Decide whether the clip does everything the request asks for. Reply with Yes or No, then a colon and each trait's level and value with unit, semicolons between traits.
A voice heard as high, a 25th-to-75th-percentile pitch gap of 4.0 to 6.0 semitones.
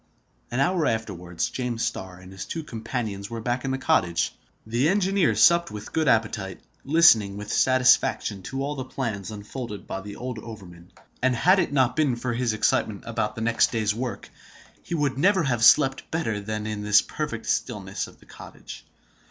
No: low, 115 Hz; average, 4.4 semitones